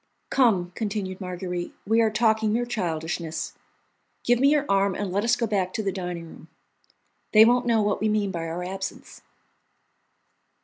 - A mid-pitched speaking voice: No, high, 200 Hz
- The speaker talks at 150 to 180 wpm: Yes, average, 170 wpm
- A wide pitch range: No, average, 3.8 semitones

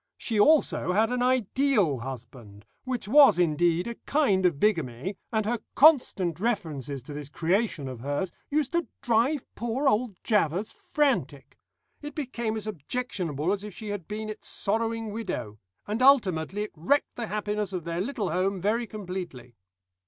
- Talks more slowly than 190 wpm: Yes, average, 160 wpm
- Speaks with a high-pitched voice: Yes, high, 205 Hz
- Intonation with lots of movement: Yes, wide, 6.1 semitones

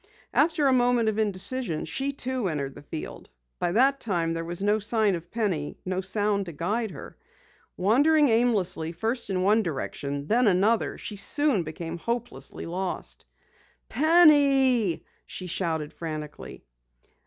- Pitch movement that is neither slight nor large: No, wide, 6.3 semitones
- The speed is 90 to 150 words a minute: Yes, average, 140 wpm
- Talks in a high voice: Yes, high, 205 Hz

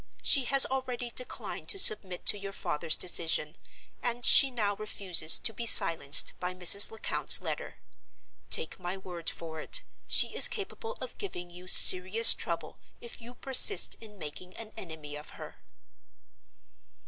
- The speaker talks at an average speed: Yes, average, 150 wpm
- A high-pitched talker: Yes, high, 195 Hz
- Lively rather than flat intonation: Yes, wide, 5.9 semitones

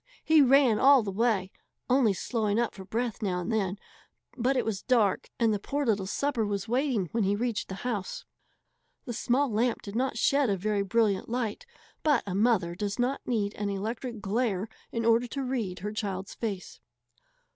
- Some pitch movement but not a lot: Yes, average, 3.6 semitones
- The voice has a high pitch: Yes, high, 220 Hz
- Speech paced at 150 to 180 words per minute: No, average, 190 wpm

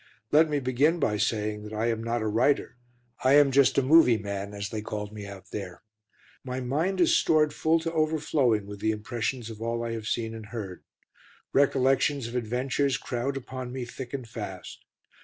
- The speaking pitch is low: Yes, low, 120 Hz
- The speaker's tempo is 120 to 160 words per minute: No, average, 195 wpm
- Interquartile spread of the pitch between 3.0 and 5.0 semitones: Yes, average, 4.4 semitones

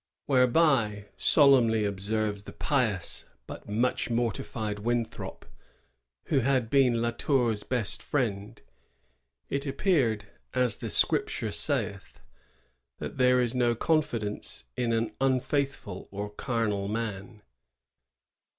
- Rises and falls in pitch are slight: No, average, 3.6 semitones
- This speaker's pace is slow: Yes, slow, 115 wpm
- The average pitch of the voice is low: Yes, low, 115 Hz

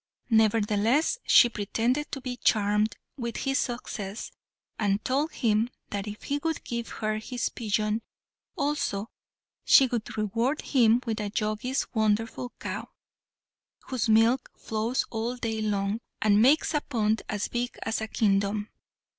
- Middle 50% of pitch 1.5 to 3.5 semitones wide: Yes, average, 2.7 semitones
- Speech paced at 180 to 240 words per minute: No, average, 140 wpm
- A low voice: No, high, 225 Hz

